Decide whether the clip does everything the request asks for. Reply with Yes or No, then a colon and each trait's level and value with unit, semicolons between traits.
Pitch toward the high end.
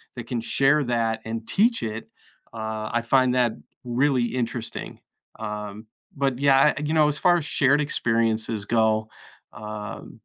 No: low, 120 Hz